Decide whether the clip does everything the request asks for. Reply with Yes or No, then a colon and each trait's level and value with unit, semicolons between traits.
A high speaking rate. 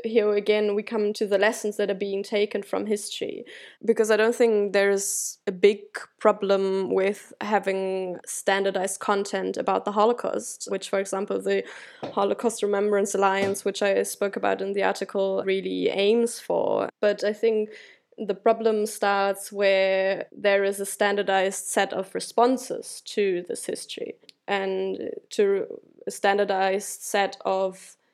No: average, 145 wpm